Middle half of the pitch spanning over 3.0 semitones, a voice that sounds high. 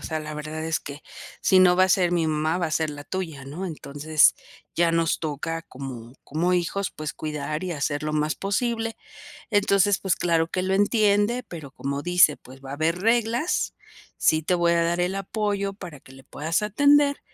No: average, 4.3 semitones; medium, 170 Hz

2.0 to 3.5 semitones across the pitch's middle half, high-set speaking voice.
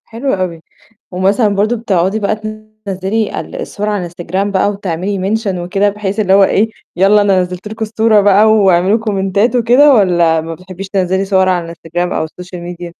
Yes: average, 2.8 semitones; high, 195 Hz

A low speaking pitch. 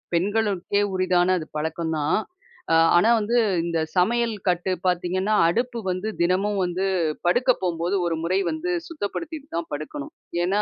No: medium, 185 Hz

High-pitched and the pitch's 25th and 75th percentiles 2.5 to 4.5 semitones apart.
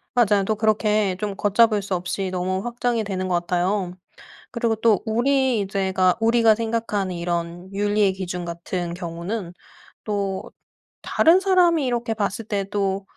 Yes: high, 200 Hz; average, 3.4 semitones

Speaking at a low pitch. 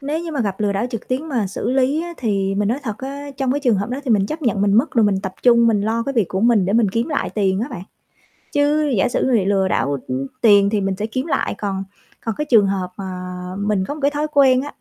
No: high, 225 Hz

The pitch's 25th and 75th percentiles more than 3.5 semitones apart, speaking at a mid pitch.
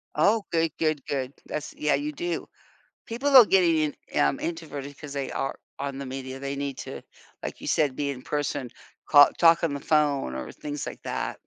No: average, 3.1 semitones; medium, 145 Hz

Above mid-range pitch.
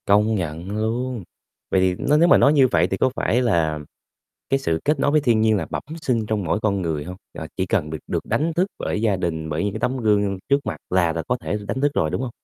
No: low, 105 Hz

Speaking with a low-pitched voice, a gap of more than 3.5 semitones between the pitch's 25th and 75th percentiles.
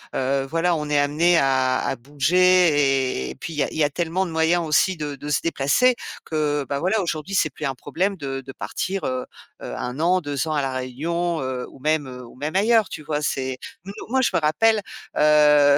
No: medium, 150 Hz; average, 4.0 semitones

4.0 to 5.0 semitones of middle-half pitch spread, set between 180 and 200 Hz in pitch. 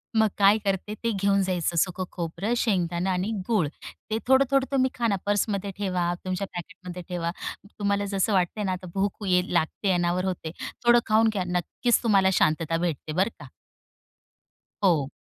No: average, 2.7 semitones; high, 190 Hz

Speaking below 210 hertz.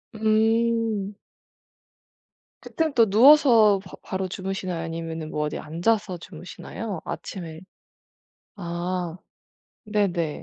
Yes: high, 190 Hz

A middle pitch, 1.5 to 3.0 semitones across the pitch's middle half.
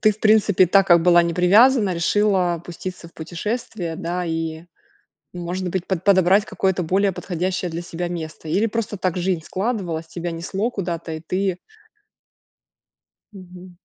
Yes: medium, 180 Hz; narrow, 2.6 semitones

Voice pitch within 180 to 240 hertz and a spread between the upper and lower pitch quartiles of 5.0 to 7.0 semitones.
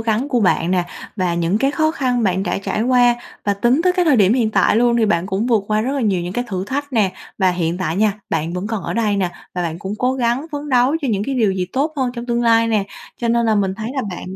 No: high, 225 Hz; average, 4.6 semitones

